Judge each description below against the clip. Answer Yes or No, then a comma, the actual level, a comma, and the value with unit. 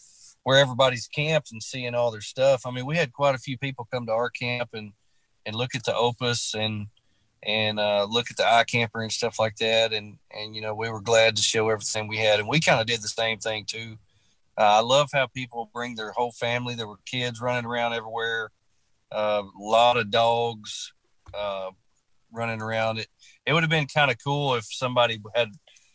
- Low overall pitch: Yes, low, 115 Hz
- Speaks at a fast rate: Yes, fast, 215 wpm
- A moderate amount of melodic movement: No, narrow, 2.2 semitones